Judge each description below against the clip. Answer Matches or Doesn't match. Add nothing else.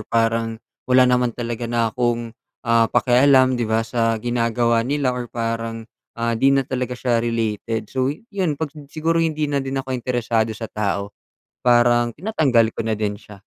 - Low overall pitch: Matches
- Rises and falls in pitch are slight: Matches